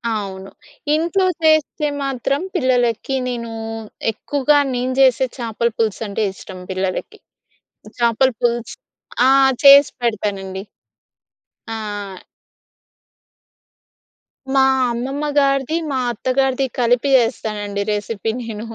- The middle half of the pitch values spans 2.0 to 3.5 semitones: No, average, 4.0 semitones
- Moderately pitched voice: No, high, 240 Hz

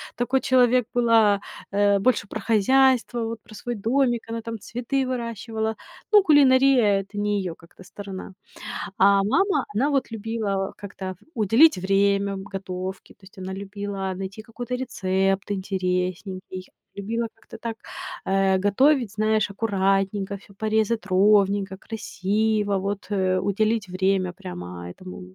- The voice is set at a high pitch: Yes, high, 205 Hz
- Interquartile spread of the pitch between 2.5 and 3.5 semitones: Yes, average, 3.1 semitones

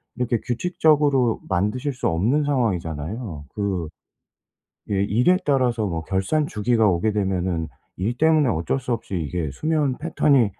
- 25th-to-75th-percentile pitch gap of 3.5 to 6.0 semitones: No, wide, 6.6 semitones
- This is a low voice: Yes, low, 115 Hz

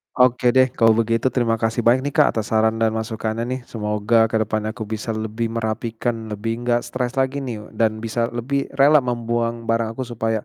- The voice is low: Yes, low, 115 Hz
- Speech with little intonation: Yes, narrow, 1.6 semitones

